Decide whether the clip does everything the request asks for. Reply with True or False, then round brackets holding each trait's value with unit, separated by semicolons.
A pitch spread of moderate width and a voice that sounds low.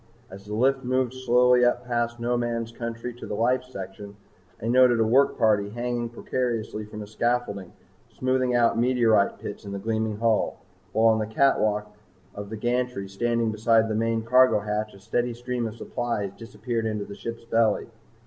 False (2.3 semitones; 115 Hz)